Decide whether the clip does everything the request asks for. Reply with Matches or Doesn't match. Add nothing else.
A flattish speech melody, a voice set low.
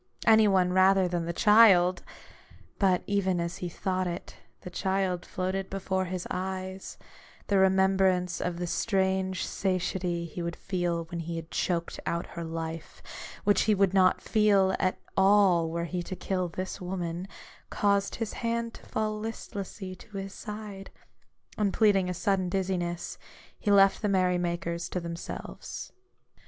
Doesn't match